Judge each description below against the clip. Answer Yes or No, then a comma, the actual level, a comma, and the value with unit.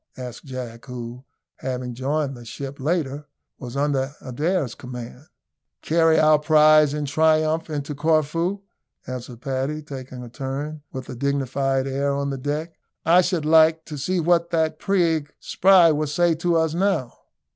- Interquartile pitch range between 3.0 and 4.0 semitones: Yes, average, 3.3 semitones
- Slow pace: No, average, 155 wpm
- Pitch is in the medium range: Yes, medium, 145 Hz